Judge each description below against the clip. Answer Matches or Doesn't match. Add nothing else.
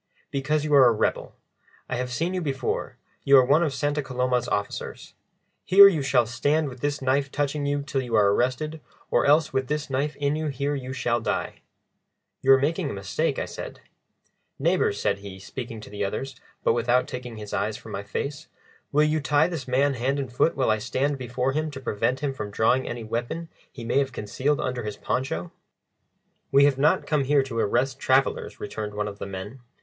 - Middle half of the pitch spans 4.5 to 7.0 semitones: Doesn't match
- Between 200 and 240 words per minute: Matches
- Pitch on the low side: Matches